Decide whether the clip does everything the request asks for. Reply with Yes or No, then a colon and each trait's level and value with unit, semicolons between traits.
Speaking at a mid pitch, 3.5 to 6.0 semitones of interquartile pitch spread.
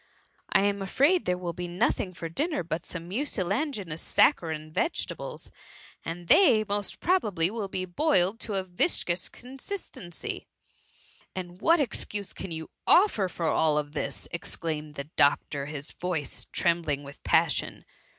Yes: medium, 180 Hz; average, 4.7 semitones